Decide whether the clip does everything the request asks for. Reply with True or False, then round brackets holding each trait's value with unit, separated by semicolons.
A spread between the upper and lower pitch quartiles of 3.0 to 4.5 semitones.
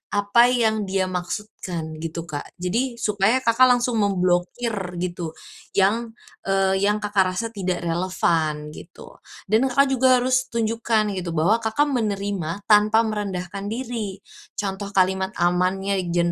True (3.9 semitones)